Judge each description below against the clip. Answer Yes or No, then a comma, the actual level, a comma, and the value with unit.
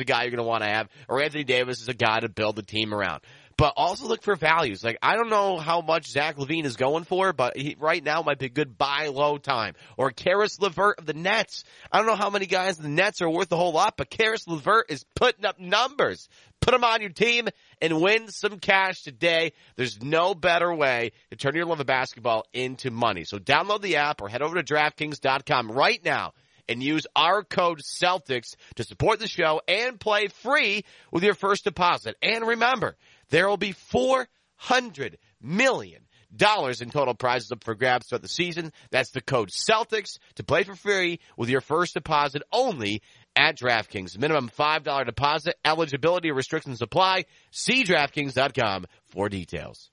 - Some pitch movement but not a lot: No, wide, 7.0 semitones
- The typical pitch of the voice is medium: Yes, medium, 150 Hz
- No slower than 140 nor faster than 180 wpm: No, average, 195 wpm